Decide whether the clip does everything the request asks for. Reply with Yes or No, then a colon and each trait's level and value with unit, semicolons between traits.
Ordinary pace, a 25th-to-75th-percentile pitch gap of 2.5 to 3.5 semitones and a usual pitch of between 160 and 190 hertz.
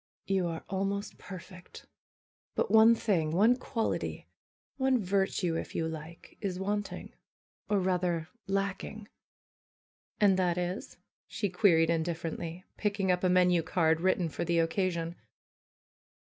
No: slow, 125 wpm; average, 2.9 semitones; medium, 185 Hz